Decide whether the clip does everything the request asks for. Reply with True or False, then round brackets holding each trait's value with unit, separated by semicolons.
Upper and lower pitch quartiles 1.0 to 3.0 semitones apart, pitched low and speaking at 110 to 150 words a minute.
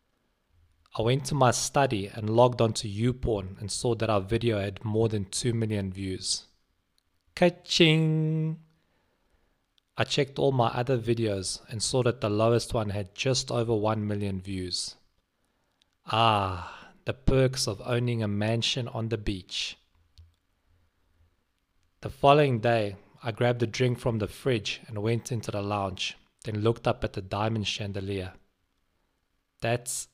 False (4.1 semitones; 110 Hz; 145 wpm)